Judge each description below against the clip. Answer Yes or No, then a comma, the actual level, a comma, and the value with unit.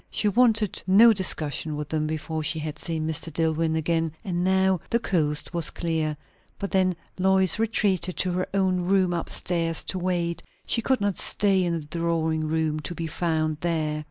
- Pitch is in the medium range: Yes, medium, 170 Hz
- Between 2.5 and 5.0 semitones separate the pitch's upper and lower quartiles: Yes, average, 3.0 semitones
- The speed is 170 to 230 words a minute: Yes, average, 185 wpm